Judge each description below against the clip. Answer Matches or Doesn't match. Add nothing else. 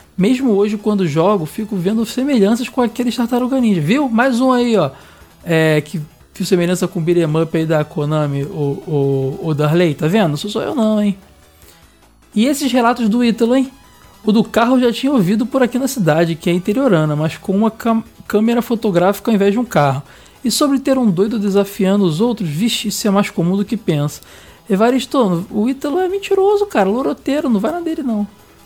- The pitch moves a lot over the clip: Matches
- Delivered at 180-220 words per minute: Matches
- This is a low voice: Doesn't match